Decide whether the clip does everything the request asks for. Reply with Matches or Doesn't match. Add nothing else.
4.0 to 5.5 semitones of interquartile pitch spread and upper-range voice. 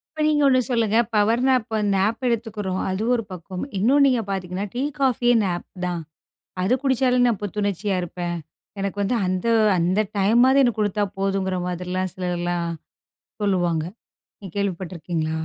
Matches